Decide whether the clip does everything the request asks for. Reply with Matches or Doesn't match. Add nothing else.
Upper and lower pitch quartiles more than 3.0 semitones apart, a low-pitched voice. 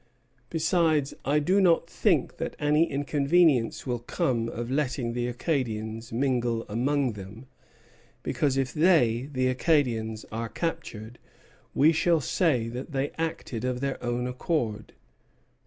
Matches